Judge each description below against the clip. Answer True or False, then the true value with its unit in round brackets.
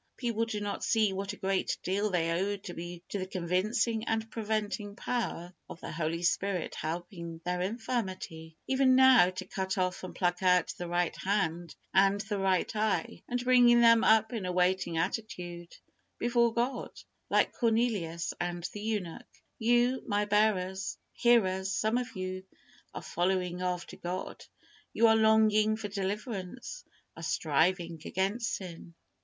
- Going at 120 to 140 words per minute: False (150 wpm)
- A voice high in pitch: True (195 Hz)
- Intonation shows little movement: False (3.9 semitones)